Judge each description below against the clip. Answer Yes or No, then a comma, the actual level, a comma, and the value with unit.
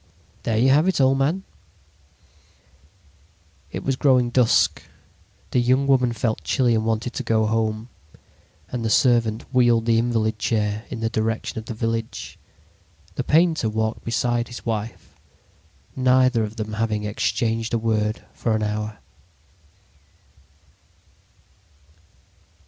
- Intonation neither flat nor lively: No, narrow, 2.3 semitones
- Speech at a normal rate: No, slow, 130 wpm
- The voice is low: Yes, low, 115 Hz